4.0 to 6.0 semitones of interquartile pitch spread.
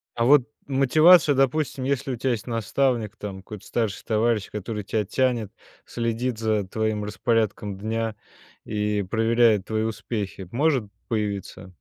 No: average, 2.7 semitones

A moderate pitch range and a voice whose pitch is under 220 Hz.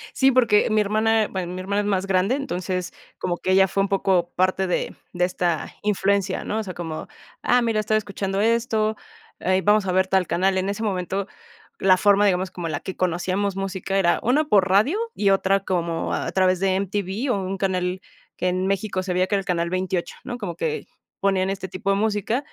No: narrow, 2.0 semitones; high, 190 Hz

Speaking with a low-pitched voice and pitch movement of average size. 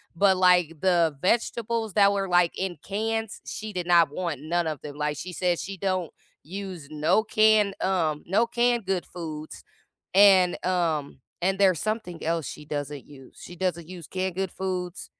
No: medium, 180 Hz; average, 3.3 semitones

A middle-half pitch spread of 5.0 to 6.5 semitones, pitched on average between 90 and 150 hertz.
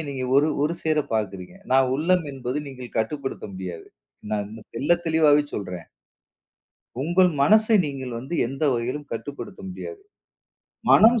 Yes: wide, 5.6 semitones; medium, 140 Hz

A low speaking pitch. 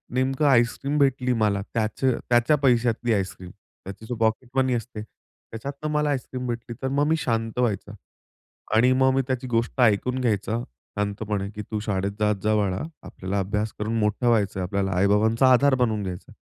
Yes: low, 115 Hz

